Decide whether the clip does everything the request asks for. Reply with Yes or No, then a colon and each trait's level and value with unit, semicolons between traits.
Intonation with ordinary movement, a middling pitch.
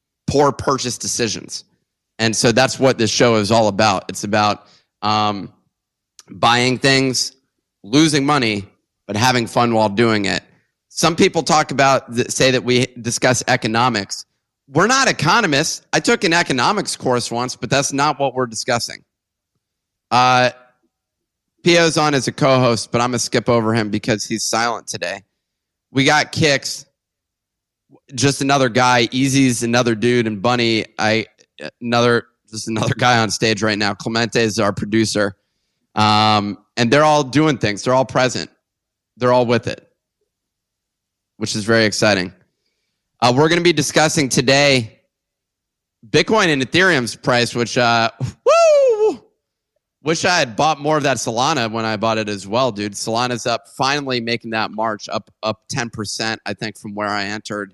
No: average, 3.7 semitones; low, 120 Hz